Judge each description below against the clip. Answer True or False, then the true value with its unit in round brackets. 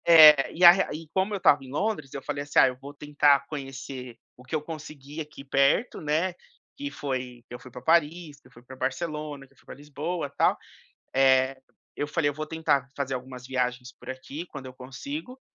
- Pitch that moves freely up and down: False (3.2 semitones)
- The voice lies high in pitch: False (145 Hz)